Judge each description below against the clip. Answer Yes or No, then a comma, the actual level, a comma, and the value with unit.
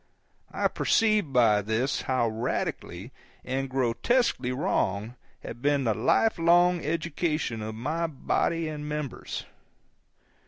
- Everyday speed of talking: No, slow, 115 wpm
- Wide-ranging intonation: Yes, wide, 6.1 semitones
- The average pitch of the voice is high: No, low, 135 Hz